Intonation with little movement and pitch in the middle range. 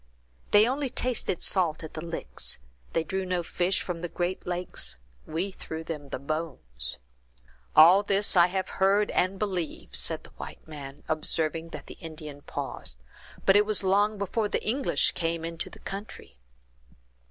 No: average, 3.7 semitones; medium, 175 Hz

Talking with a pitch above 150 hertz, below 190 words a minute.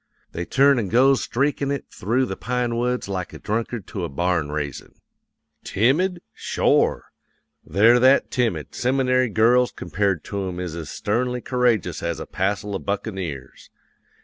No: low, 110 Hz; average, 150 wpm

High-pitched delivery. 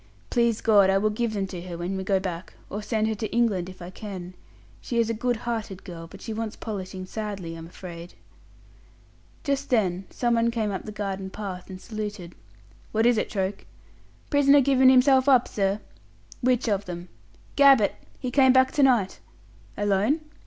Yes: high, 210 Hz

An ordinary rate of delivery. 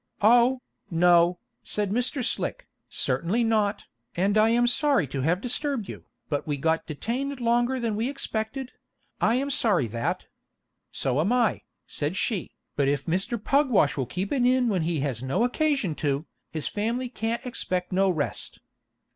Yes: average, 165 wpm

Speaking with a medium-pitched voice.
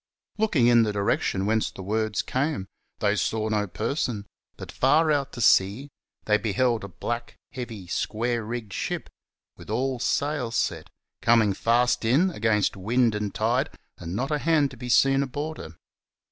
No: low, 120 Hz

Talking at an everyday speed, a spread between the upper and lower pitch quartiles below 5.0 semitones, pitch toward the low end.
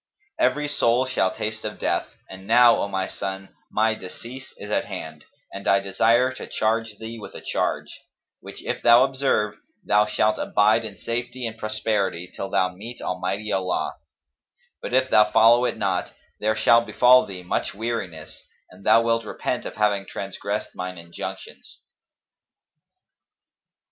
Yes: average, 155 wpm; average, 3.2 semitones; low, 110 Hz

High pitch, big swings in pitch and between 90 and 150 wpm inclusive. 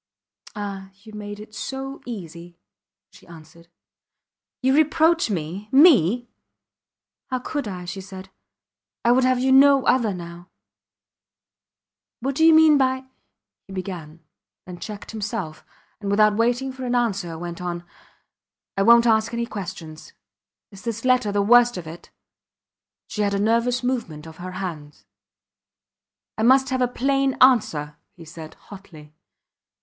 Yes: high, 210 Hz; wide, 6.2 semitones; average, 145 wpm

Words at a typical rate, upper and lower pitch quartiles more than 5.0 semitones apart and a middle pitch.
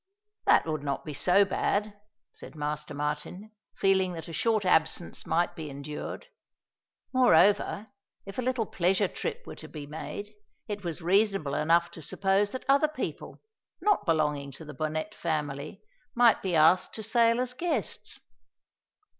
Yes: average, 155 wpm; wide, 5.6 semitones; medium, 180 Hz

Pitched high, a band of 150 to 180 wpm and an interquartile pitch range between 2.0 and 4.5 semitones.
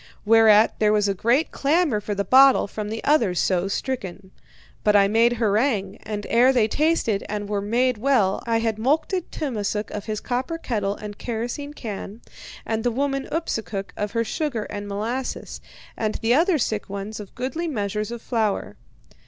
Yes: high, 225 Hz; average, 175 wpm; average, 3.9 semitones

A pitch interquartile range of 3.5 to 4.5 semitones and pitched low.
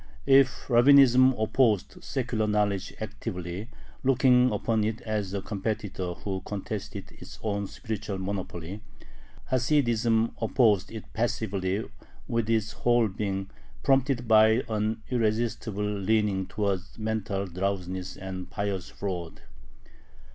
No: average, 3.1 semitones; low, 105 Hz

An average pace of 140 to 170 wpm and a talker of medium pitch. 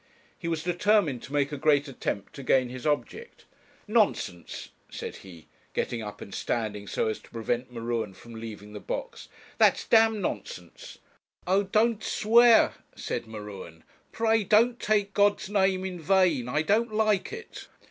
Yes: average, 160 wpm; medium, 155 Hz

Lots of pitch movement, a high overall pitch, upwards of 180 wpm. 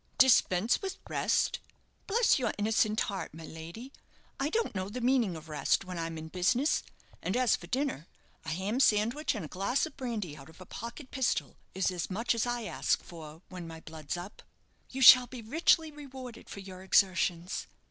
Yes: wide, 6.5 semitones; high, 210 Hz; average, 190 wpm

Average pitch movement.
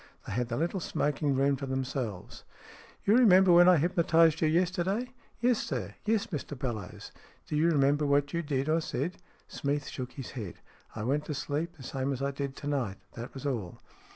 Yes: average, 4.2 semitones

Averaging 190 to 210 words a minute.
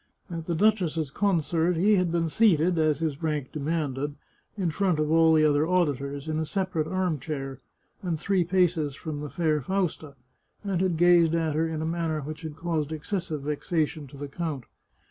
Yes: average, 195 wpm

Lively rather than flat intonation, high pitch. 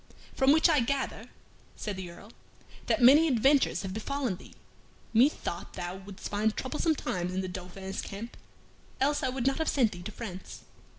Yes: wide, 6.3 semitones; high, 220 Hz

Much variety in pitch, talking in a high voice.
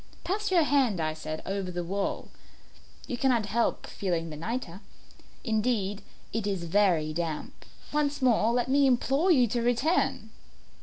Yes: wide, 6.5 semitones; high, 220 Hz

